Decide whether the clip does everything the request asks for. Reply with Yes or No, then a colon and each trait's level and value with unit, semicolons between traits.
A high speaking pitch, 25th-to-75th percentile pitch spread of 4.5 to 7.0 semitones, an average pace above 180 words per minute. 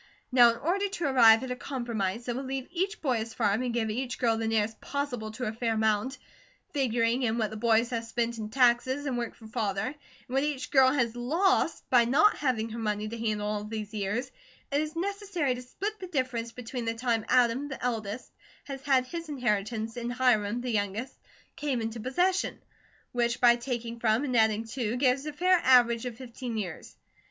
No: high, 240 Hz; average, 3.0 semitones; fast, 205 wpm